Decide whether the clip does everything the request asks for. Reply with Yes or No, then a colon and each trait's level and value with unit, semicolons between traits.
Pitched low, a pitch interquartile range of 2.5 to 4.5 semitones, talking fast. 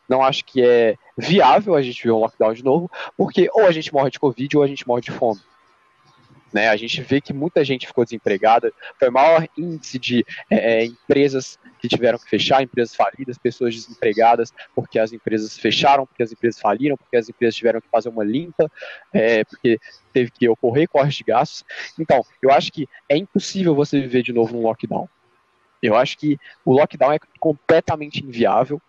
Yes: low, 130 Hz; average, 4.0 semitones; fast, 195 wpm